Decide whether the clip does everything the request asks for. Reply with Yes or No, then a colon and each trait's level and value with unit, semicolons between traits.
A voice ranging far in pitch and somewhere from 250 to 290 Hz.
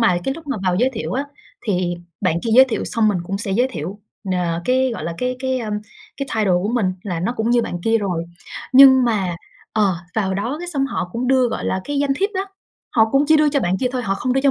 No: wide, 5.7 semitones; high, 230 Hz